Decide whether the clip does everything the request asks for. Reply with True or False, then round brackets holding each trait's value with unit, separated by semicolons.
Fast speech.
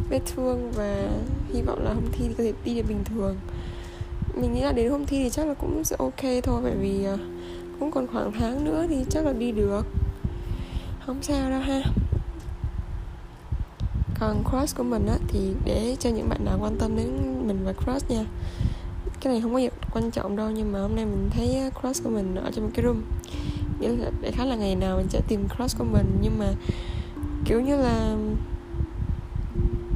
False (205 wpm)